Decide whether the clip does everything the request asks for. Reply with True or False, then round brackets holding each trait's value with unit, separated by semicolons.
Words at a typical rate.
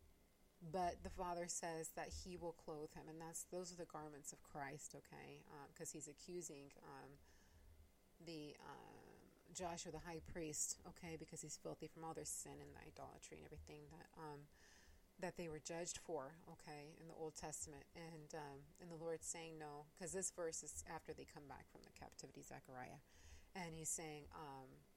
True (185 wpm)